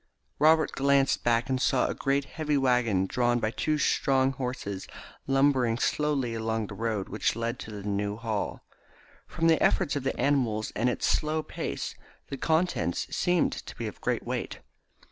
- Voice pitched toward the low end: Yes, low, 125 Hz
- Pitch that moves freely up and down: No, average, 4.1 semitones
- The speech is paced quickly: No, average, 170 wpm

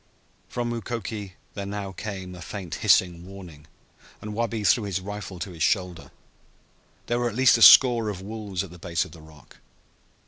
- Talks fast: No, average, 180 wpm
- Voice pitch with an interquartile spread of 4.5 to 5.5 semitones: No, average, 3.6 semitones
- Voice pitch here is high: No, low, 100 Hz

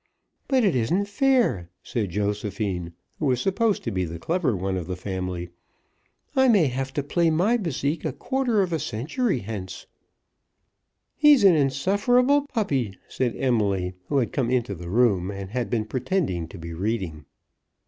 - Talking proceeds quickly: No, average, 165 wpm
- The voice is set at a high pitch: No, low, 125 Hz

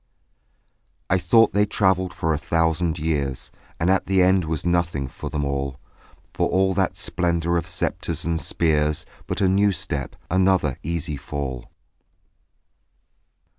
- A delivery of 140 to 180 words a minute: Yes, average, 145 wpm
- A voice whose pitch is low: Yes, very low, 85 Hz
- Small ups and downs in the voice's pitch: No, average, 3.8 semitones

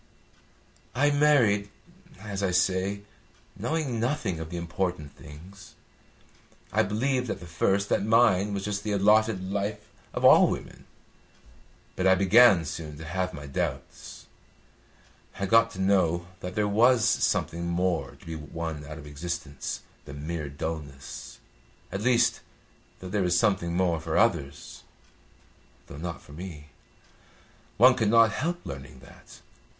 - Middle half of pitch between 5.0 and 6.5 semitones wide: No, average, 4.6 semitones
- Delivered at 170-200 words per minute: No, average, 145 wpm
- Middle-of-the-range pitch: No, very low, 95 Hz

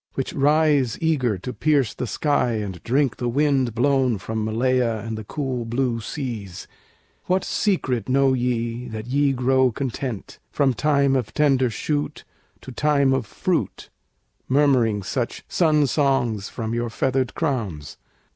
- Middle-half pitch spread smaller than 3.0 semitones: No, average, 3.4 semitones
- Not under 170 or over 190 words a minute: No, average, 145 wpm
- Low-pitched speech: Yes, low, 130 Hz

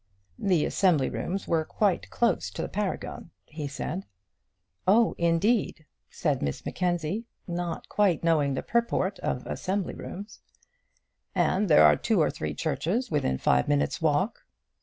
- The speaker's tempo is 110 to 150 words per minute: Yes, average, 140 wpm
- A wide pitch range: No, average, 4.7 semitones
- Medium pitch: Yes, medium, 175 Hz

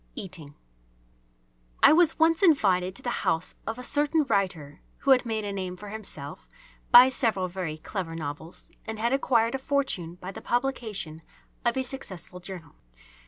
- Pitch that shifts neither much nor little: No, wide, 6.6 semitones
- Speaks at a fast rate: No, average, 165 wpm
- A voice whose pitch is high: Yes, high, 200 Hz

